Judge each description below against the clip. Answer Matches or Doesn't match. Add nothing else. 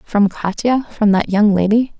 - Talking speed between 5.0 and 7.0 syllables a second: Doesn't match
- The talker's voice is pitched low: Doesn't match